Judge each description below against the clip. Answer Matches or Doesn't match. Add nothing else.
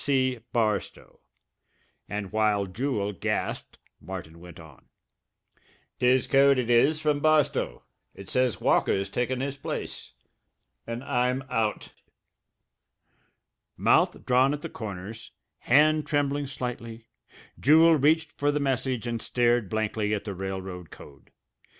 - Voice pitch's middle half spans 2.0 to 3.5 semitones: Doesn't match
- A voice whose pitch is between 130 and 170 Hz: Doesn't match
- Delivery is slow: Matches